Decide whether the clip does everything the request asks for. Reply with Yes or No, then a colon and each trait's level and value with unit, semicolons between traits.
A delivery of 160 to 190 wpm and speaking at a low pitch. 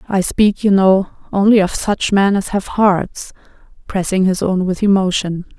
No: average, 170 wpm; high, 195 Hz